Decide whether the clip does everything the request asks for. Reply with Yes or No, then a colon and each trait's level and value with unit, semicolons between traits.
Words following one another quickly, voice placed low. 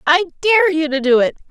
No: fast, 240 wpm; very high, 290 Hz